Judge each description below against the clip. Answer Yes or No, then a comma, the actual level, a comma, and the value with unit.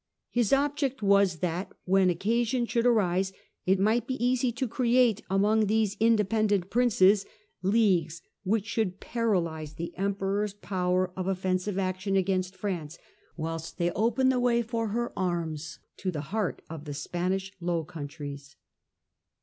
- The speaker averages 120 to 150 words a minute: Yes, average, 140 wpm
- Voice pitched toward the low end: No, high, 195 Hz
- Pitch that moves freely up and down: No, average, 4.0 semitones